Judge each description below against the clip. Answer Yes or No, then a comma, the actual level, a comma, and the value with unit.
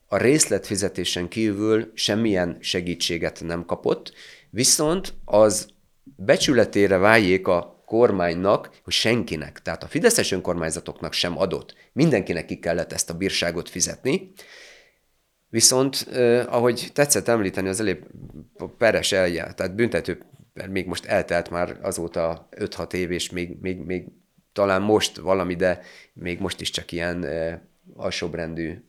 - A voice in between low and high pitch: No, very low, 95 Hz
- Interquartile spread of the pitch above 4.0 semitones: Yes, average, 4.5 semitones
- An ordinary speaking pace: Yes, average, 130 wpm